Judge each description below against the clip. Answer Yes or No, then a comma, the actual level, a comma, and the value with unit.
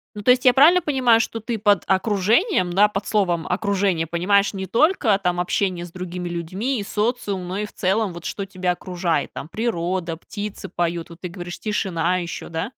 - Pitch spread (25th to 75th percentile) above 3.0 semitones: Yes, average, 3.4 semitones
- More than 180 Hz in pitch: Yes, high, 190 Hz